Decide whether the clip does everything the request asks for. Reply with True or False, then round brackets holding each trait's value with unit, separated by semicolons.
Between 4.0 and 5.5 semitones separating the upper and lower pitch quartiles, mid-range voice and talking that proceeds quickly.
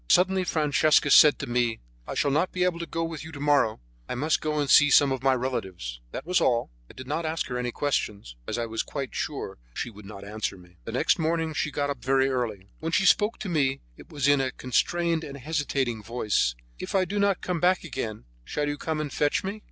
True (5.0 semitones; 145 Hz; 240 wpm)